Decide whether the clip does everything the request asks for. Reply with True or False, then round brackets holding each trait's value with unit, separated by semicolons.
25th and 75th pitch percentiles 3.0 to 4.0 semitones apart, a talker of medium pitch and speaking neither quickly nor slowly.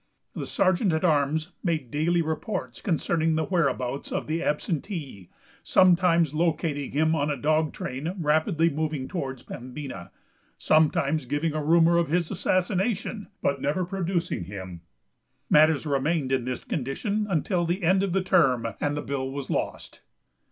True (3.5 semitones; 160 Hz; 150 wpm)